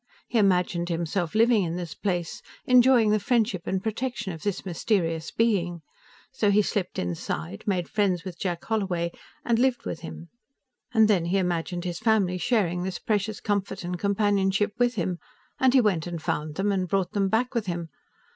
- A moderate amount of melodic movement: Yes, average, 3.7 semitones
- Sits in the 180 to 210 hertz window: Yes, high, 190 Hz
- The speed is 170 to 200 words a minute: Yes, average, 180 wpm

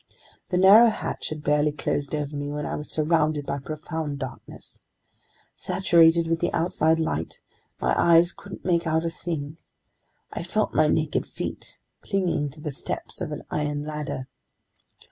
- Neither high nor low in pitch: Yes, medium, 155 Hz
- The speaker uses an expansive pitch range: No, narrow, 2.4 semitones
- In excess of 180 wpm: No, average, 160 wpm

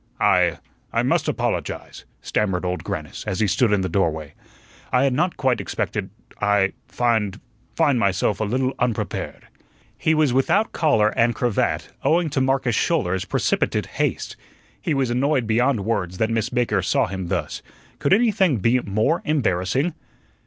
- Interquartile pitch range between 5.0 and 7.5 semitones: Yes, wide, 5.4 semitones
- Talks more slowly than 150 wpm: No, average, 155 wpm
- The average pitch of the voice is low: Yes, low, 120 Hz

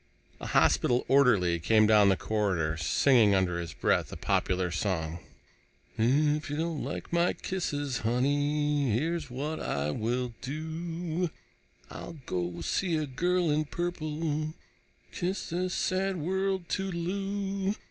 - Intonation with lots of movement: Yes, wide, 7.9 semitones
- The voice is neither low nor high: Yes, medium, 150 Hz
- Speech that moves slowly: Yes, slow, 130 wpm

